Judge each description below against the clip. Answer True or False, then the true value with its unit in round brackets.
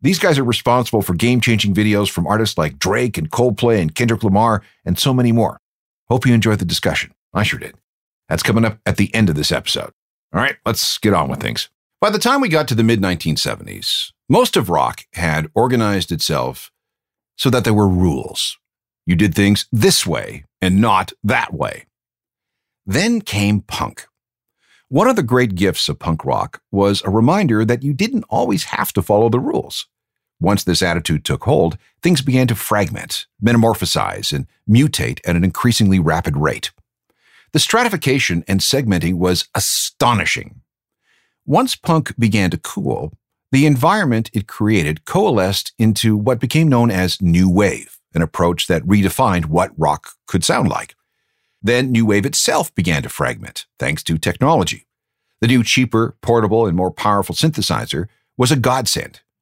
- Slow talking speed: False (170 wpm)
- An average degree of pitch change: True (5.0 semitones)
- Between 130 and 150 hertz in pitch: False (110 Hz)